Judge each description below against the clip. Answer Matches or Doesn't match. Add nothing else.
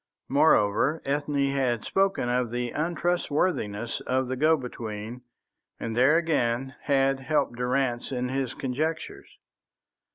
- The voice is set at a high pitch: Doesn't match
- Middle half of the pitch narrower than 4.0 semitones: Matches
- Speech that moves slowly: Matches